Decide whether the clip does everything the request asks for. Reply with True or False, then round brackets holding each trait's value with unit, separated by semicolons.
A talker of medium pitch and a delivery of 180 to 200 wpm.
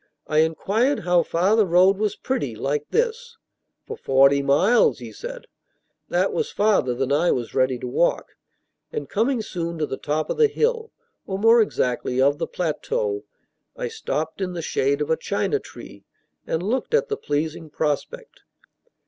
False (180 Hz; 170 wpm)